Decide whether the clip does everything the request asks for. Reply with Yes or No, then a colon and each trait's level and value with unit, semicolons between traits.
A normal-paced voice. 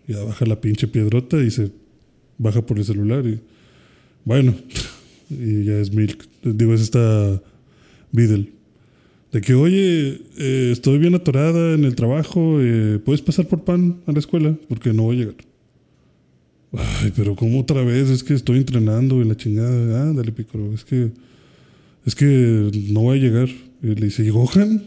Yes: average, 175 wpm